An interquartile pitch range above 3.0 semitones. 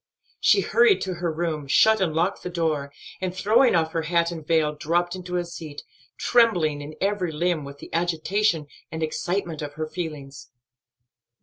No: narrow, 2.6 semitones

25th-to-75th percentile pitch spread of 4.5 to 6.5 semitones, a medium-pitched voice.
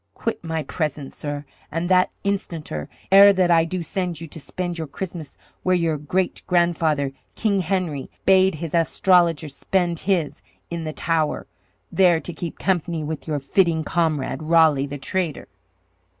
No: average, 3.0 semitones; medium, 165 Hz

